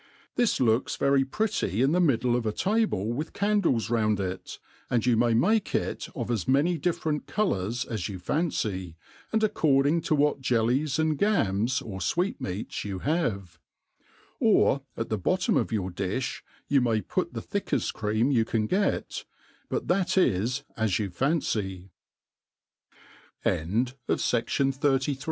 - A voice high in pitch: No, low, 125 Hz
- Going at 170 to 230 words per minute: No, average, 140 wpm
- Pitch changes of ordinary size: No, wide, 6.8 semitones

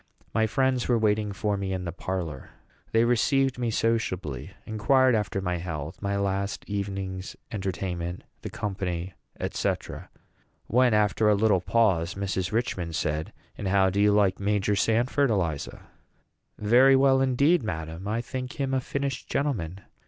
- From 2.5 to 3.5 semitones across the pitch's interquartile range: No, average, 4.2 semitones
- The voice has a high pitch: No, low, 100 Hz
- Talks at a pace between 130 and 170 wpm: Yes, average, 150 wpm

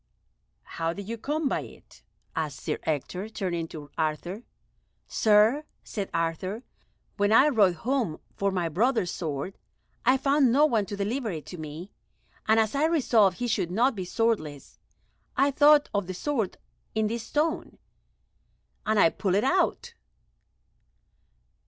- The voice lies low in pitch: No, high, 210 Hz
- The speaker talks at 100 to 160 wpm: Yes, average, 150 wpm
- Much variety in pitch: Yes, wide, 6.5 semitones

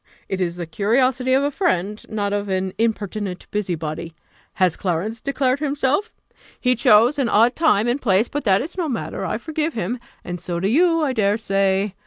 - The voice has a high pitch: Yes, high, 215 Hz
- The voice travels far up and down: Yes, wide, 5.8 semitones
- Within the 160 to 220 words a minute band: Yes, average, 190 wpm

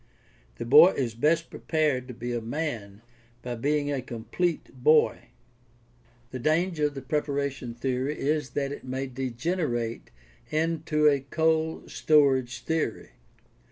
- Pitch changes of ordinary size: Yes, average, 3.8 semitones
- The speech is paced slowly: Yes, slow, 130 wpm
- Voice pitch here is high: No, medium, 140 Hz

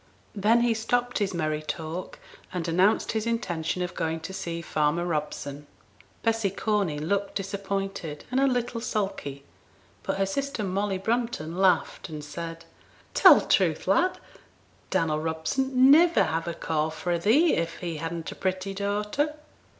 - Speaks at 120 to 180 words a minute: Yes, average, 150 wpm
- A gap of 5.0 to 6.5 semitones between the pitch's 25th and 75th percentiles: Yes, average, 5.3 semitones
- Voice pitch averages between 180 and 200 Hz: Yes, high, 190 Hz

